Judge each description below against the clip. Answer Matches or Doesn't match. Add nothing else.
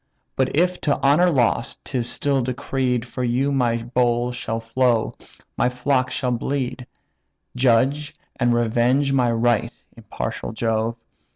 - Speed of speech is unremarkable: Doesn't match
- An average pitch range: Doesn't match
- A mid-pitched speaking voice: Doesn't match